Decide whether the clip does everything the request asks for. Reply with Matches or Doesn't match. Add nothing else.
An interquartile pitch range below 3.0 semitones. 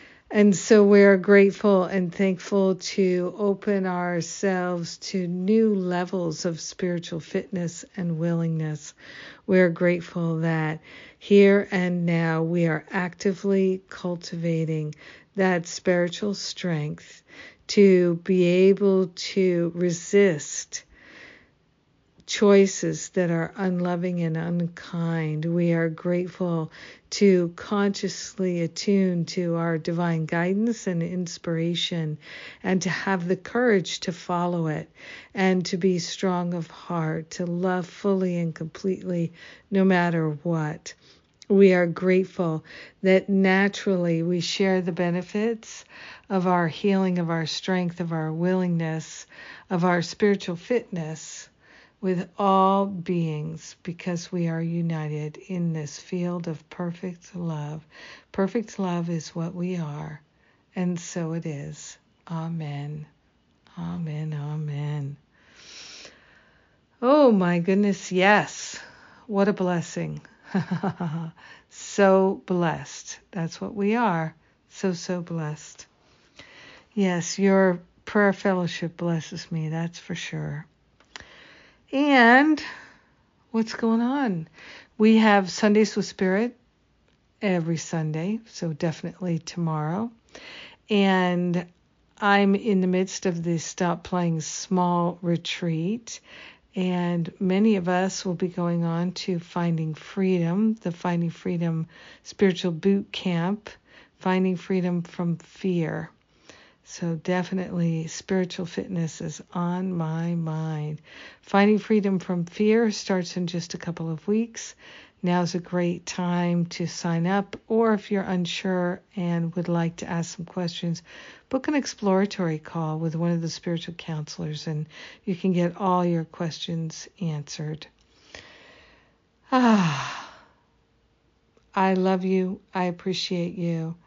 Matches